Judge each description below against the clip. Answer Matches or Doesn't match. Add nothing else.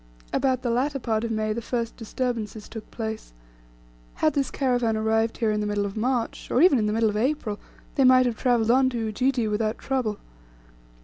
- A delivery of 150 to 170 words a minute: Doesn't match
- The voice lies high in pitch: Matches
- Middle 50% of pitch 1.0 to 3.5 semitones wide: Matches